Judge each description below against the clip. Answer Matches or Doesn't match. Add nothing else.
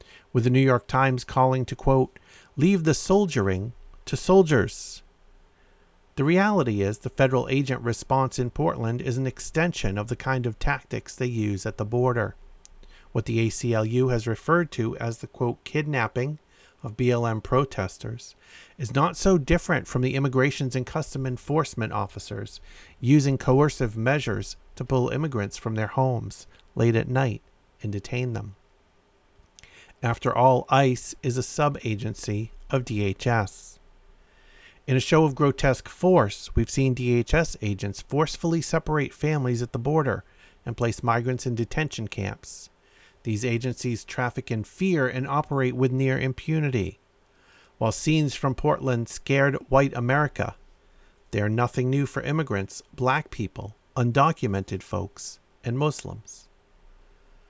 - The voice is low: Matches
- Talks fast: Doesn't match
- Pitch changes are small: Doesn't match